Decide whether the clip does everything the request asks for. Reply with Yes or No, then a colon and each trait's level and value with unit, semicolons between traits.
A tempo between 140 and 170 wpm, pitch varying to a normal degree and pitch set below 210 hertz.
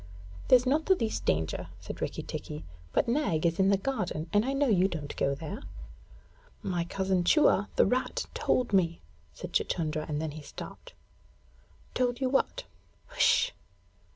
No: average, 165 wpm; wide, 8.2 semitones; high, 190 Hz